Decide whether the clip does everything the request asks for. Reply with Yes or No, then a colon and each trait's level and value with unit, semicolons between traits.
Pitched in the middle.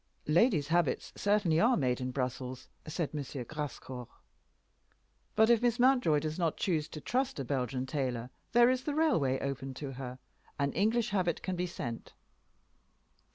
Yes: medium, 155 Hz